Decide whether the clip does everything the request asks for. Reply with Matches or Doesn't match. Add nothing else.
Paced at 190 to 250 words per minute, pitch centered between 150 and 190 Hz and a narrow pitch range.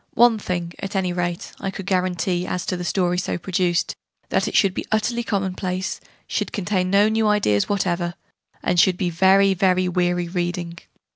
Doesn't match